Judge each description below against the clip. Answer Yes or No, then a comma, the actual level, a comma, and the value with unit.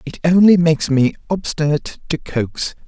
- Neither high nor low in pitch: Yes, medium, 155 Hz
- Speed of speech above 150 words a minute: No, average, 145 wpm